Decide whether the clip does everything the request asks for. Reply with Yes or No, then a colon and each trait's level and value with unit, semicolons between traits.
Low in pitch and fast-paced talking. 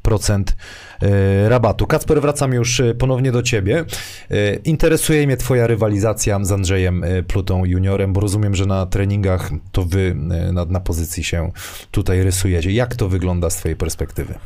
No: low, 100 Hz; average, 145 wpm